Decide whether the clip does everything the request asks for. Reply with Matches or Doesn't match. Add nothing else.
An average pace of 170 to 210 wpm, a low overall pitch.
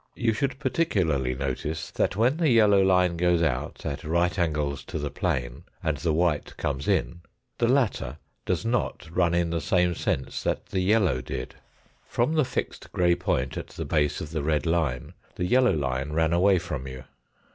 Matches